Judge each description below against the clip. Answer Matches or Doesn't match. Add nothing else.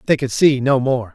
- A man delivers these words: Matches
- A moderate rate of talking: Doesn't match